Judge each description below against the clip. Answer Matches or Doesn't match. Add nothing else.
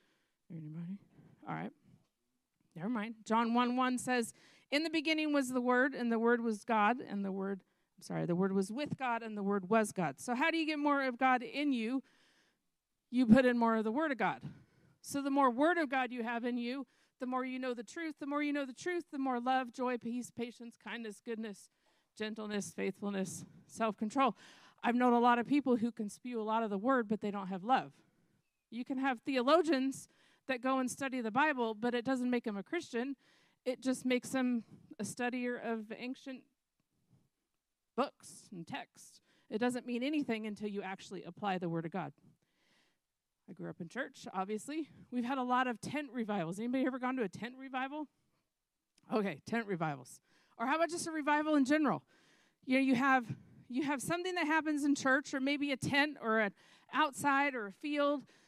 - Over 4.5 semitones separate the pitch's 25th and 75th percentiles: Doesn't match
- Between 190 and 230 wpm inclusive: Matches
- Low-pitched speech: Doesn't match